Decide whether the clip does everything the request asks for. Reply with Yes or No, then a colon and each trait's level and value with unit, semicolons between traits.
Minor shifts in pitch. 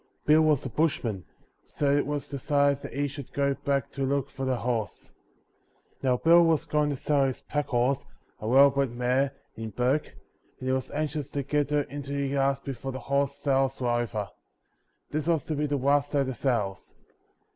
Yes: narrow, 1.8 semitones